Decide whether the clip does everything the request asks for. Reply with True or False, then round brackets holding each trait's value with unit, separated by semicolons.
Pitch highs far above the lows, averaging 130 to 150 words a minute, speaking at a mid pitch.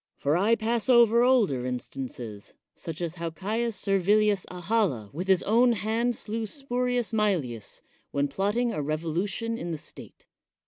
False (6.3 semitones; 145 wpm; 200 Hz)